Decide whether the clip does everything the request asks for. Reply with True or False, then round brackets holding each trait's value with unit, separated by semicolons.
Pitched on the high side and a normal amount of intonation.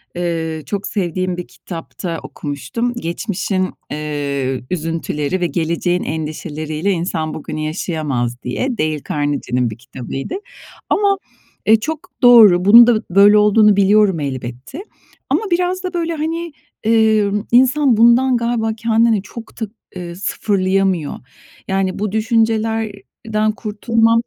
False (195 Hz; 6.2 semitones)